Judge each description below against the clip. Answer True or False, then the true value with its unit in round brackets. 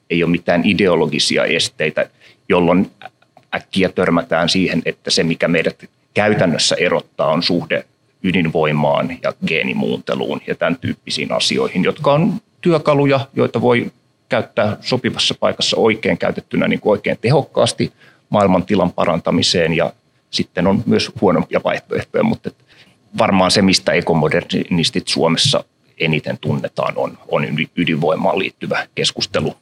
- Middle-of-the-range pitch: False (120 Hz)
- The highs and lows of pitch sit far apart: True (8.2 semitones)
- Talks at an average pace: True (120 wpm)